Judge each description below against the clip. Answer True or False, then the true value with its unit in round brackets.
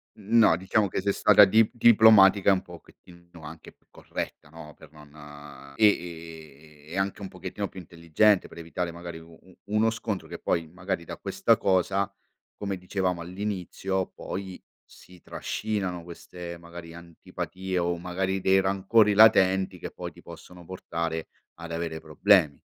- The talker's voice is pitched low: True (90 Hz)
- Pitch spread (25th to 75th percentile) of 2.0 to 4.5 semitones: True (2.7 semitones)